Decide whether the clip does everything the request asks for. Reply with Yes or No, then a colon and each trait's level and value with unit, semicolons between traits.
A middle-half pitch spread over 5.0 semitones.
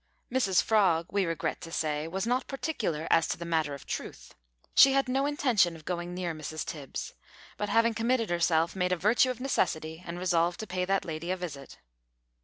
Yes: wide, 5.4 semitones